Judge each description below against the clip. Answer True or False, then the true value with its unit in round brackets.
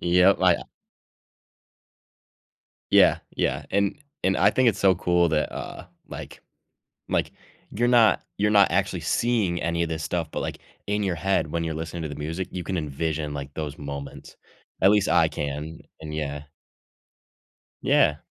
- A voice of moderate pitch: False (85 Hz)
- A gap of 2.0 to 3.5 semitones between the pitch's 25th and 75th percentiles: False (4.1 semitones)